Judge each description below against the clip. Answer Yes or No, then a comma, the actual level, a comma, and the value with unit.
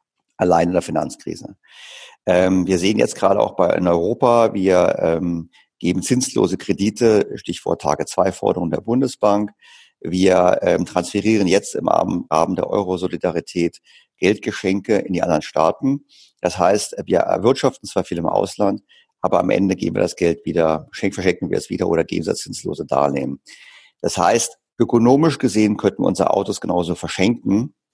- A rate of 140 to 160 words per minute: Yes, average, 150 wpm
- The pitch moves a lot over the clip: Yes, wide, 6.2 semitones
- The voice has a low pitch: Yes, low, 105 Hz